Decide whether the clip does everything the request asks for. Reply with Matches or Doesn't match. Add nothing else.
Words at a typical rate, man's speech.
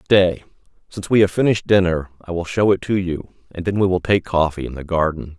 Doesn't match